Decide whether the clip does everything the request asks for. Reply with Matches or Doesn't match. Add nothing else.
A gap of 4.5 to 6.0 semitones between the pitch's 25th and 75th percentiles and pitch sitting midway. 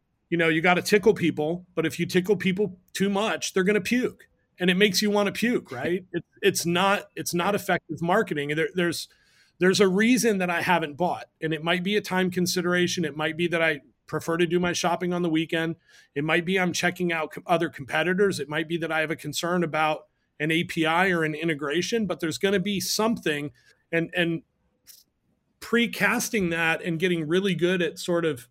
Doesn't match